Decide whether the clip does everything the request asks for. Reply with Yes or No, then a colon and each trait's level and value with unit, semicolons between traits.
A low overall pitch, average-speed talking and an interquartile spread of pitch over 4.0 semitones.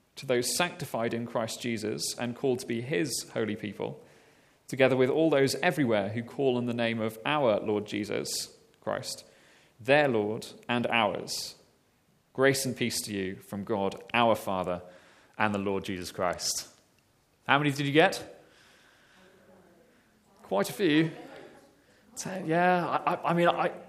Yes: low, 120 Hz; average, 150 wpm; average, 5.2 semitones